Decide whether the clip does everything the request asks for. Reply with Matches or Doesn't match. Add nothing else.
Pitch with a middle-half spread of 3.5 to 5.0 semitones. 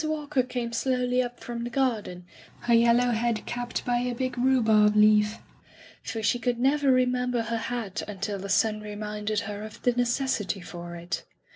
Doesn't match